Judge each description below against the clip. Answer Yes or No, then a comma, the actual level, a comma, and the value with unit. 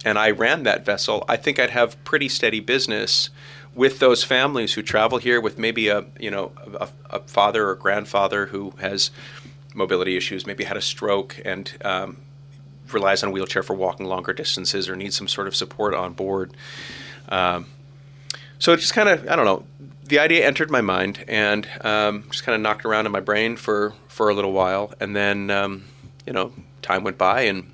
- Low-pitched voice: Yes, low, 110 Hz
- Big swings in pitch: Yes, wide, 5.8 semitones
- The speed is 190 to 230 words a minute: Yes, average, 200 wpm